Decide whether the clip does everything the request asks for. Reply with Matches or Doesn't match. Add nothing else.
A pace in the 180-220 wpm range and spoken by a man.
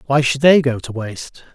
Doesn't match